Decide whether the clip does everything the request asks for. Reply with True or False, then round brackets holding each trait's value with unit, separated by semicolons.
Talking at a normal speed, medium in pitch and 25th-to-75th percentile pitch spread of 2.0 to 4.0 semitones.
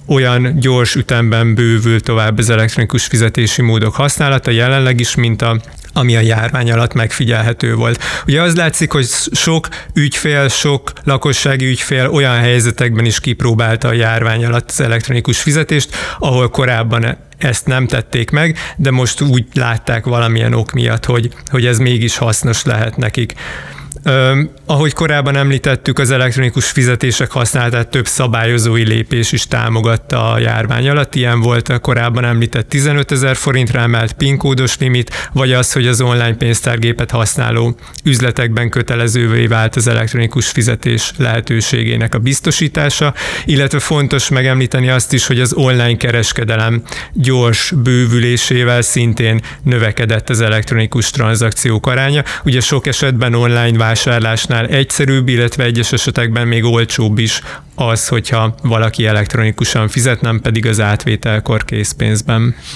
False (135 wpm; 120 Hz; 2.5 semitones)